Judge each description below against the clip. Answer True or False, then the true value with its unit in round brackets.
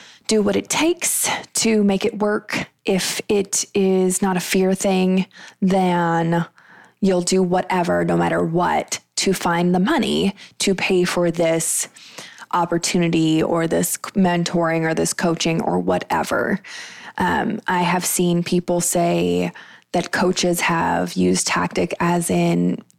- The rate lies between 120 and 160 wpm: True (135 wpm)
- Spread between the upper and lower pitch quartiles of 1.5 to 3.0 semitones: True (2.7 semitones)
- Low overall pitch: False (180 Hz)